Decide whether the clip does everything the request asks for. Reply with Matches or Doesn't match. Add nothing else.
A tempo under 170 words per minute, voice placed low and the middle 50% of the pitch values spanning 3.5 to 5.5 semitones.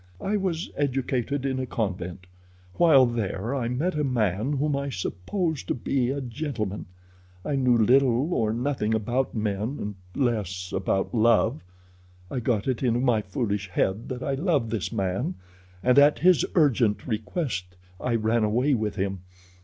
Matches